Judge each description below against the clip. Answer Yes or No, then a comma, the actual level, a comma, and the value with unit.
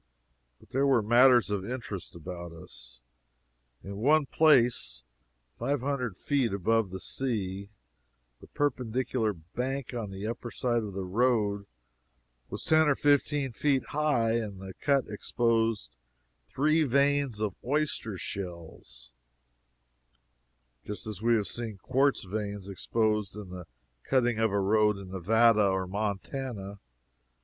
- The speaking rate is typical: No, slow, 130 wpm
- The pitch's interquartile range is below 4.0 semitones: No, average, 4.8 semitones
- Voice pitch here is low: Yes, low, 110 Hz